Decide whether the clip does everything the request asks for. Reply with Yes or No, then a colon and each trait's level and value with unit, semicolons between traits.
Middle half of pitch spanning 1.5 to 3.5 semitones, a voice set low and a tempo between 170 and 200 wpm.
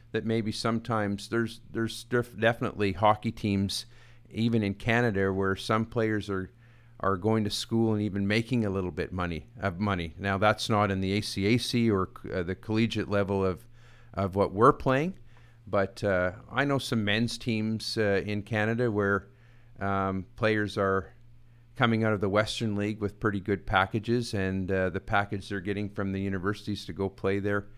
Yes: average, 2.8 semitones; low, 105 Hz; average, 175 wpm